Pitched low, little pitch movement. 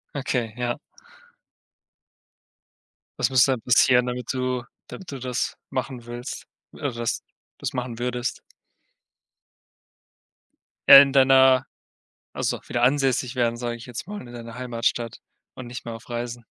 Yes: low, 125 Hz; narrow, 1.6 semitones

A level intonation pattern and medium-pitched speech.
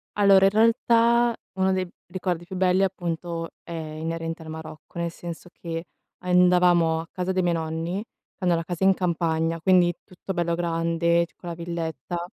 Yes: narrow, 1.9 semitones; medium, 175 Hz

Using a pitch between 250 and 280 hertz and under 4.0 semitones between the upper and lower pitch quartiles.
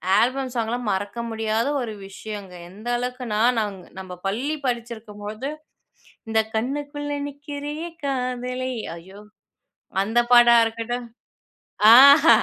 No: high, 240 Hz; average, 3.5 semitones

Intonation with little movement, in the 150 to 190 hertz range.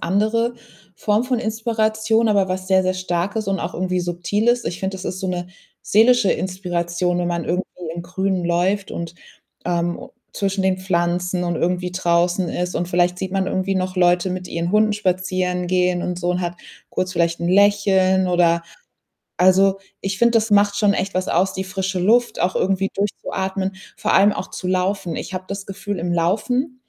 Yes: narrow, 2.1 semitones; medium, 185 Hz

